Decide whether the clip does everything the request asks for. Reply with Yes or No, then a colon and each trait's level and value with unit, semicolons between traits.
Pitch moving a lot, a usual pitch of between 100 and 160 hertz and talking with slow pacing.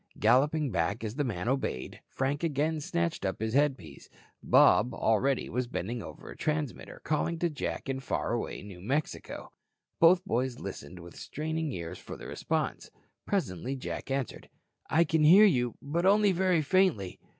No: wide, 6.2 semitones; low, 135 Hz; average, 160 wpm